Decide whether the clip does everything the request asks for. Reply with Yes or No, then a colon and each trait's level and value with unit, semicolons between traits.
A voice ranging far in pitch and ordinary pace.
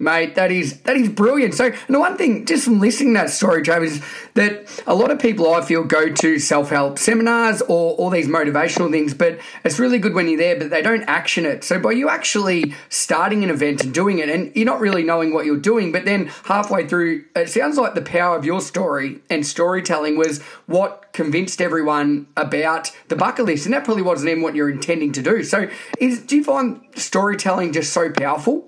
No: wide, 5.9 semitones; fast, 220 wpm